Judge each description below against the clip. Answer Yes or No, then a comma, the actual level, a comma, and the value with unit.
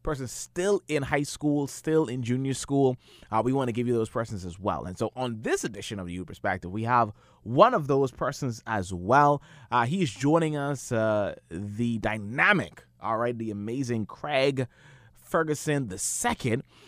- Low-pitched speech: Yes, low, 125 Hz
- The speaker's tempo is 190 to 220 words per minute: No, average, 180 wpm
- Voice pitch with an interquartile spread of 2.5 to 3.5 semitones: No, average, 4.8 semitones